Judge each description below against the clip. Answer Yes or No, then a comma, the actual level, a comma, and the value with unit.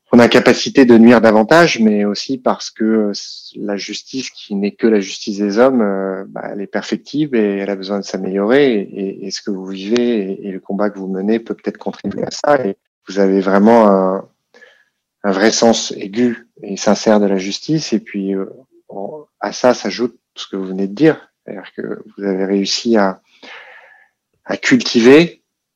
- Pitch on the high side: No, low, 105 Hz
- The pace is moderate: Yes, average, 180 wpm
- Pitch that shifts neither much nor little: Yes, average, 3.0 semitones